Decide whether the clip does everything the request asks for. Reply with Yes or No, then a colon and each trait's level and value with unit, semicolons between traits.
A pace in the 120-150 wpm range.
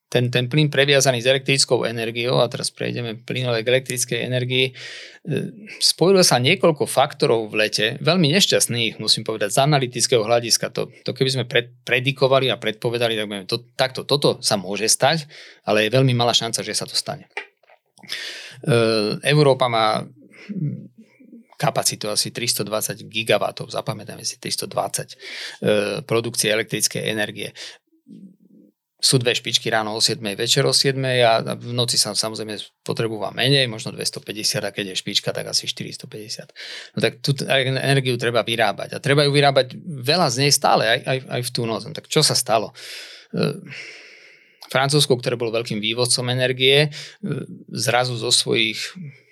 Yes: average, 145 wpm